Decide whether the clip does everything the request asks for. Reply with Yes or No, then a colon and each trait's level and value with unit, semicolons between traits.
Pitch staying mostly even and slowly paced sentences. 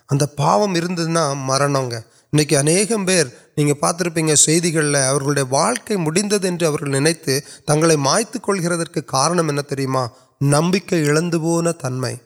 No: average, 3.4 semitones; slow, 75 wpm